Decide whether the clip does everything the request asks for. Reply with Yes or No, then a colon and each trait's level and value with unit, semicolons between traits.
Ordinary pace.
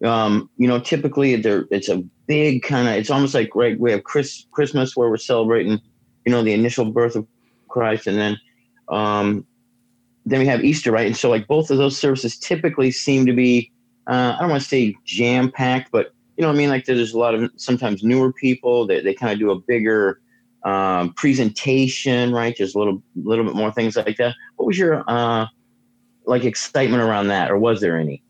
No: fast, 210 wpm